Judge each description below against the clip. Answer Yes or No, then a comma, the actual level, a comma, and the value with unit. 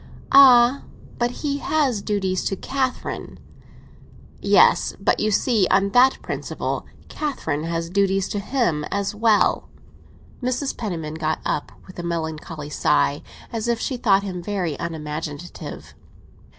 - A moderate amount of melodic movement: No, wide, 6.5 semitones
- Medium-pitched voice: No, high, 195 Hz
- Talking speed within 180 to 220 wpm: No, slow, 135 wpm